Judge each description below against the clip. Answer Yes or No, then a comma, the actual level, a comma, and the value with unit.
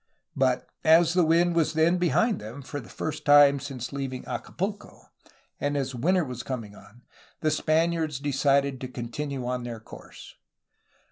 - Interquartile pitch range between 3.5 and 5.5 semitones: Yes, average, 4.2 semitones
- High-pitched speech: No, medium, 140 Hz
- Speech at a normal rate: Yes, average, 160 wpm